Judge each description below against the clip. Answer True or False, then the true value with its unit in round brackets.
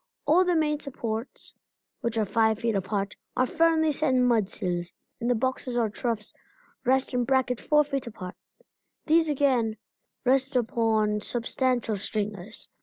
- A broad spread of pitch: False (3.9 semitones)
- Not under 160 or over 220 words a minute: False (145 wpm)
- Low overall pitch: False (240 Hz)